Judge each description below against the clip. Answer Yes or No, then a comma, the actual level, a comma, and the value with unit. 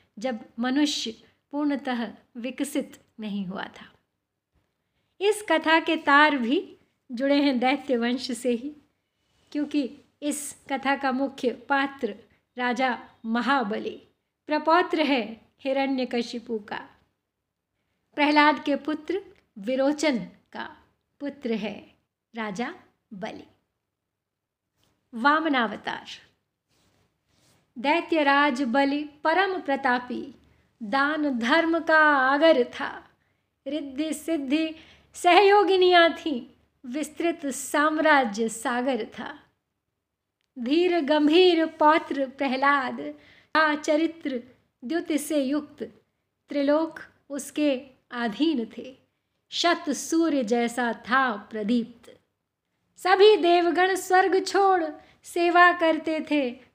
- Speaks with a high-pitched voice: Yes, very high, 285 Hz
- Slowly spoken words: Yes, slow, 90 wpm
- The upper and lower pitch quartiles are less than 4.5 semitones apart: Yes, average, 4.0 semitones